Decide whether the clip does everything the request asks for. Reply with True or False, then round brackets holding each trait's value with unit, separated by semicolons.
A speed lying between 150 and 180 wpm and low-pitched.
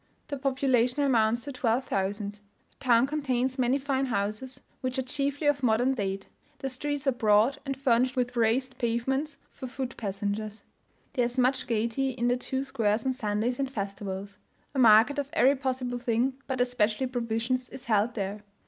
False (170 wpm; 250 Hz)